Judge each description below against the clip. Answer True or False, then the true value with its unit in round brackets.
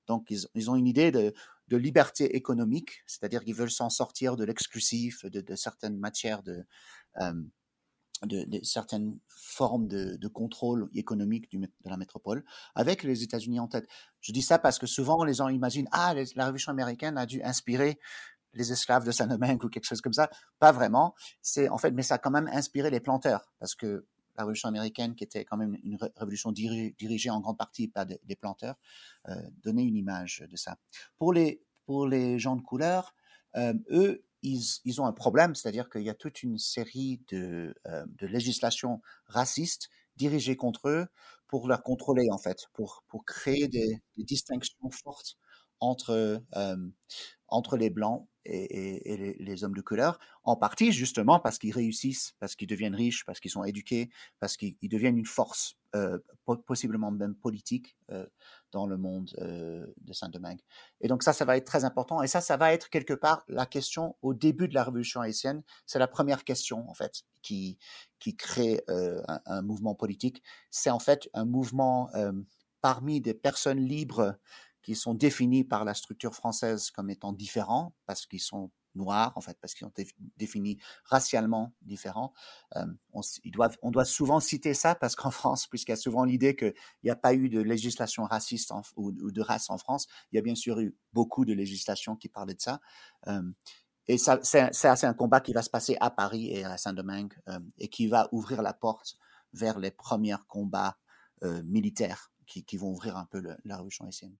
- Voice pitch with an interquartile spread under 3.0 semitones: False (3.9 semitones)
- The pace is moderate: True (200 wpm)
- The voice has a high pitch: False (120 Hz)